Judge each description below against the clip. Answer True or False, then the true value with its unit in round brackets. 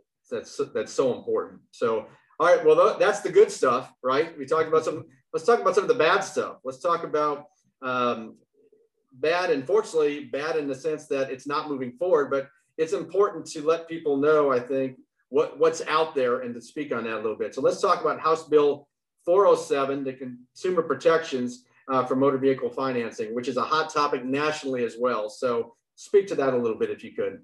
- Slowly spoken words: False (205 wpm)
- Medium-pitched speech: True (160 Hz)